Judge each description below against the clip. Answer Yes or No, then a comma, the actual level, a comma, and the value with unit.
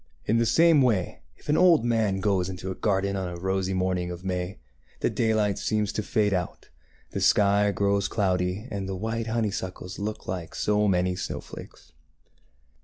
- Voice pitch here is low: Yes, low, 100 Hz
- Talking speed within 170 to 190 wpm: Yes, average, 175 wpm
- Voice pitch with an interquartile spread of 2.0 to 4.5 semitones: Yes, narrow, 2.6 semitones